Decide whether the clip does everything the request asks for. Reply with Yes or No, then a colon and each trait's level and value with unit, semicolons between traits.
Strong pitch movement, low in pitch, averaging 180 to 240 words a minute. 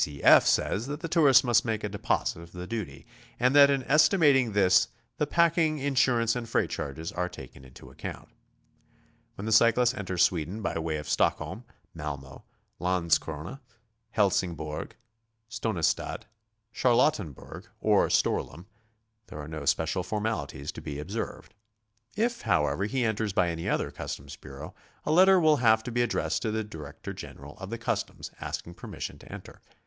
No: wide, 7.3 semitones; low, 105 Hz; average, 160 wpm